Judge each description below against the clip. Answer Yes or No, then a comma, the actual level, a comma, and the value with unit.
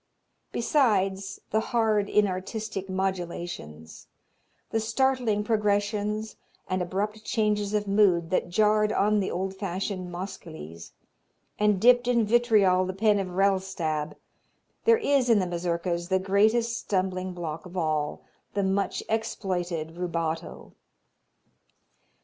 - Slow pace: Yes, slow, 115 wpm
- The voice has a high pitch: Yes, high, 195 Hz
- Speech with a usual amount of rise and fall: Yes, average, 3.2 semitones